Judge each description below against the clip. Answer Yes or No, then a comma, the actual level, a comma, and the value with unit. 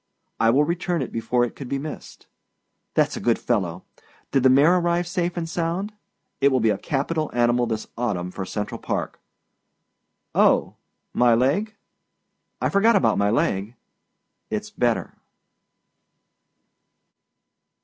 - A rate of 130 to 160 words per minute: Yes, average, 140 wpm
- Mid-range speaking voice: No, low, 130 Hz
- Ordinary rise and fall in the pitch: No, wide, 6.9 semitones